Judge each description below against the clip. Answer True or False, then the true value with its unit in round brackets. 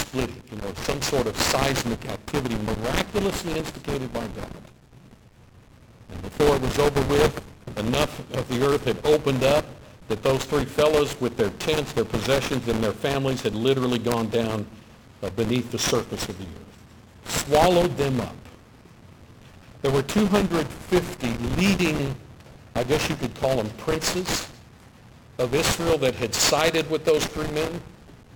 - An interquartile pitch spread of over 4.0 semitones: True (4.7 semitones)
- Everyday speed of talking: True (150 wpm)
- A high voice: False (130 Hz)